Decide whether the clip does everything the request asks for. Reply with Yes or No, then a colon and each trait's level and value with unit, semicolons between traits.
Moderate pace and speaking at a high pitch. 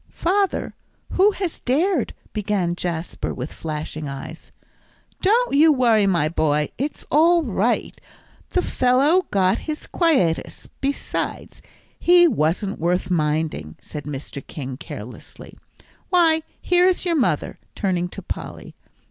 No: slow, 125 wpm; high, 210 Hz